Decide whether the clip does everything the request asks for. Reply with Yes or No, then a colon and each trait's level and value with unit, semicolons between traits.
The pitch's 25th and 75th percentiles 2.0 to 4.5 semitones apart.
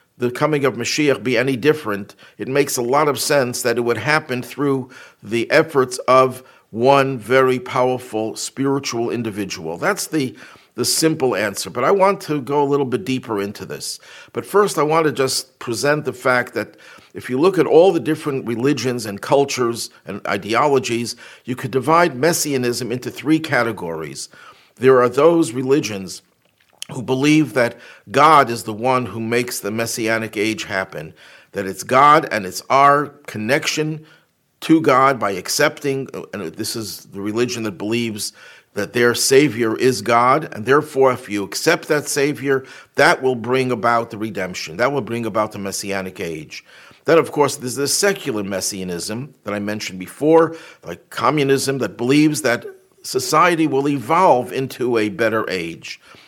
Yes: average, 3.8 semitones